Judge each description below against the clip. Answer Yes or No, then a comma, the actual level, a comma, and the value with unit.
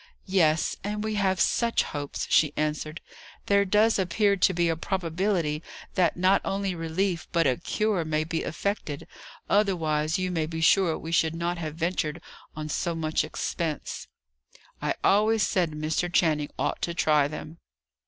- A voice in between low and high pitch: Yes, medium, 170 Hz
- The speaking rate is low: No, average, 160 wpm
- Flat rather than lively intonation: No, average, 3.7 semitones